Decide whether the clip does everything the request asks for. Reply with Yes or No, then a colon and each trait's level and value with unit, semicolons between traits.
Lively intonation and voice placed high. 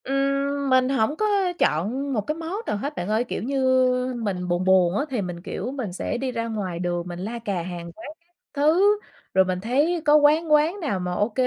Yes: wide, 7.6 semitones; high, 235 Hz